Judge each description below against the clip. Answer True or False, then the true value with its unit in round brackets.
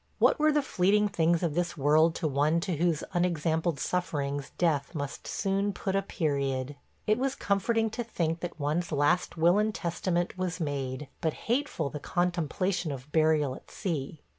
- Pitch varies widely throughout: False (4.1 semitones)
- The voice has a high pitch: False (170 Hz)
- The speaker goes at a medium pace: True (170 wpm)